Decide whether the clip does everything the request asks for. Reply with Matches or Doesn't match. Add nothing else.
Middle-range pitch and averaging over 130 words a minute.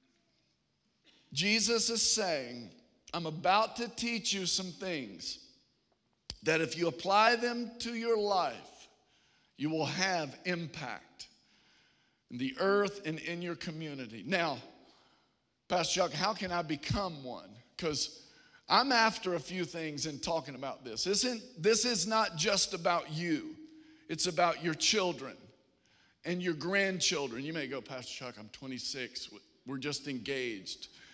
Matches